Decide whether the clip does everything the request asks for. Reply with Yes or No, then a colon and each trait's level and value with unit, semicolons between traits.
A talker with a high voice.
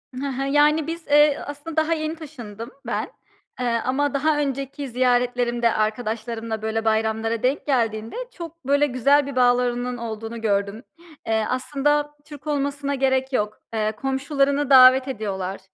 Yes: very high, 255 Hz